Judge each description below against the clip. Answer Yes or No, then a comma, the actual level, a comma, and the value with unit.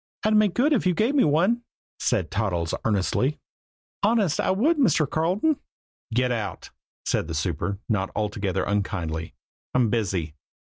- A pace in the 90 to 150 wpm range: Yes, average, 145 wpm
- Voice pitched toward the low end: Yes, low, 120 Hz